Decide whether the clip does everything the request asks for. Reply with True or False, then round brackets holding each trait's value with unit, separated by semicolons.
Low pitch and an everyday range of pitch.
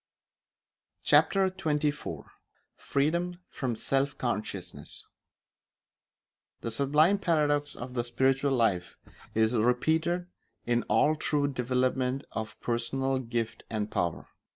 True (130 Hz; 4.2 semitones)